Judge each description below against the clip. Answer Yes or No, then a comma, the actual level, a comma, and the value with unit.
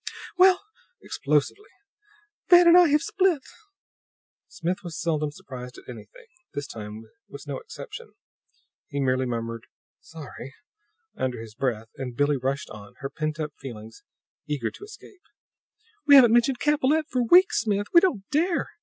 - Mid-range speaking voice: Yes, medium, 155 Hz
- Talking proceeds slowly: No, average, 145 wpm